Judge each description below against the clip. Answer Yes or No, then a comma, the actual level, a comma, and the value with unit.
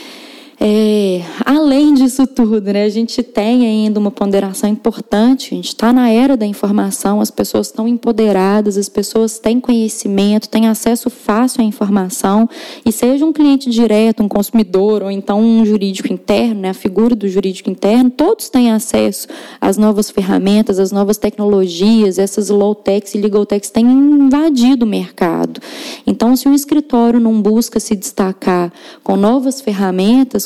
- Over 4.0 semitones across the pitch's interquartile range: No, average, 3.0 semitones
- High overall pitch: Yes, high, 220 Hz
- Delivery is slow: No, average, 155 wpm